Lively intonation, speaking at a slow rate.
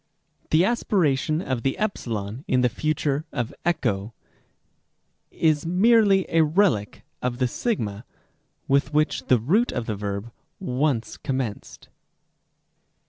Yes: wide, 6.0 semitones; slow, 120 wpm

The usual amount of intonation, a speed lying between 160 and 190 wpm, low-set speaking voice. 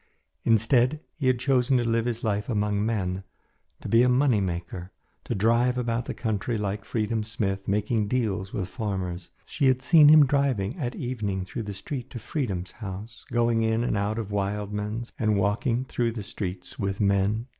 Yes: average, 3.3 semitones; average, 180 wpm; low, 110 Hz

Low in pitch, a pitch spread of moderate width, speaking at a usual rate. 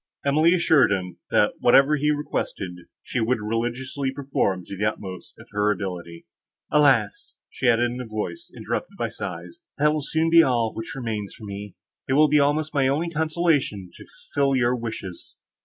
No: low, 125 Hz; wide, 6.1 semitones; average, 175 wpm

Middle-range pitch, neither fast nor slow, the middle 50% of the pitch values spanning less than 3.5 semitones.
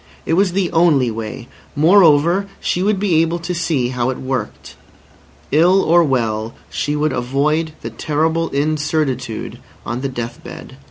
No: medium, 150 Hz; average, 155 wpm; average, 4.8 semitones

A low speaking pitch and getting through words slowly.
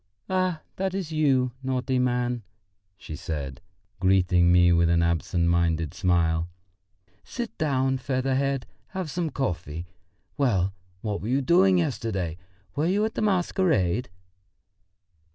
Yes: low, 125 Hz; slow, 125 wpm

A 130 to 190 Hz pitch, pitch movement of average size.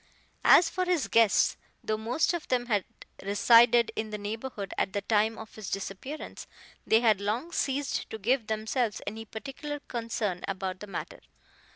No: high, 220 Hz; average, 3.5 semitones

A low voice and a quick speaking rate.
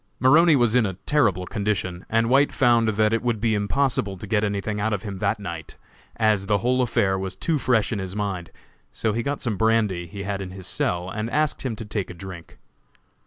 Yes: low, 105 Hz; fast, 220 wpm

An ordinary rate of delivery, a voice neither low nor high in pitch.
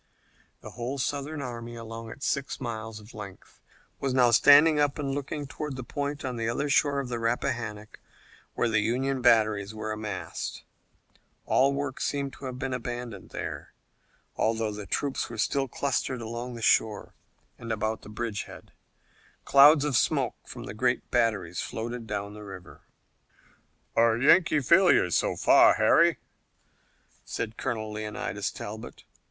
No: average, 155 wpm; low, 120 Hz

